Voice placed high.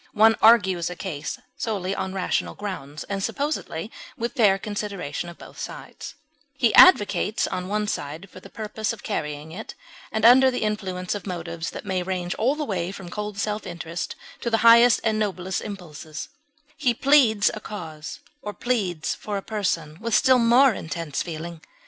Yes: high, 200 Hz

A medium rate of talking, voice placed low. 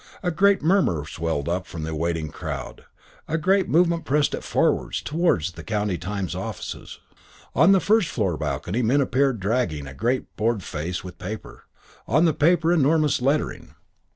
Yes: average, 165 wpm; low, 125 Hz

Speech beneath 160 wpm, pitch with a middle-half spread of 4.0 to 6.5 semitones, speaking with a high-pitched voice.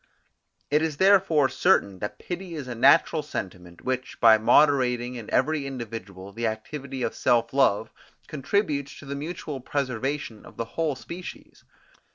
No: average, 150 wpm; average, 4.7 semitones; low, 135 Hz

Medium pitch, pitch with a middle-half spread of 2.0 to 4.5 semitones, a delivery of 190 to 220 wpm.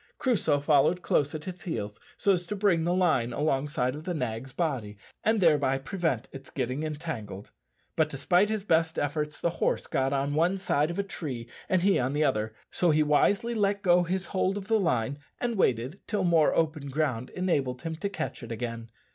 No: medium, 155 Hz; wide, 5.4 semitones; average, 200 wpm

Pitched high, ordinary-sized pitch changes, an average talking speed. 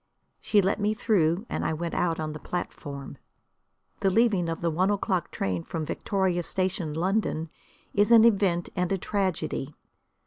No: medium, 180 Hz; average, 3.7 semitones; average, 165 wpm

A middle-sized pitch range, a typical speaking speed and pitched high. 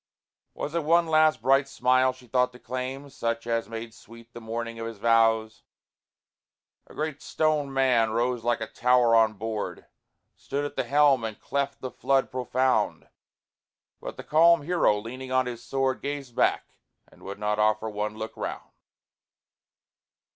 No: average, 3.2 semitones; average, 160 wpm; low, 125 Hz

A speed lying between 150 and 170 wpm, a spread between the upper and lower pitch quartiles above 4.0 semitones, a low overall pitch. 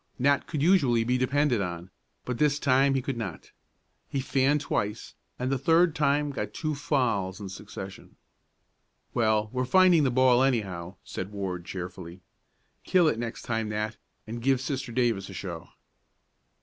Yes: average, 160 wpm; wide, 5.5 semitones; low, 125 Hz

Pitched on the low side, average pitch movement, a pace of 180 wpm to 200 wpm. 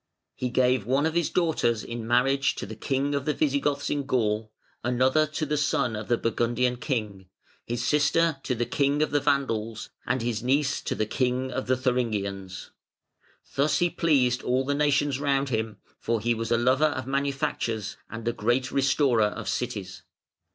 Yes: low, 130 Hz; average, 3.6 semitones; average, 185 wpm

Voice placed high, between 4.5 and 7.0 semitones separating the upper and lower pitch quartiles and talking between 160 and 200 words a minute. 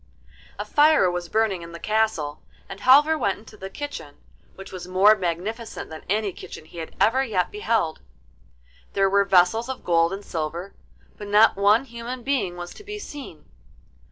Yes: high, 200 Hz; average, 4.8 semitones; average, 175 wpm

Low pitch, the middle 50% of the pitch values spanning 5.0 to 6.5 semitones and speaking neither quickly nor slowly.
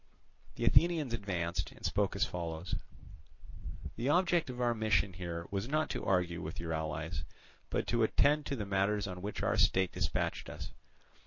Yes: low, 100 Hz; wide, 5.6 semitones; average, 170 wpm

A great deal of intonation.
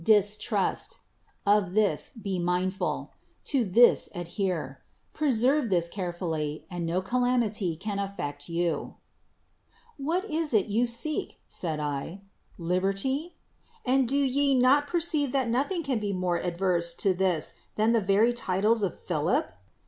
Yes: wide, 6.1 semitones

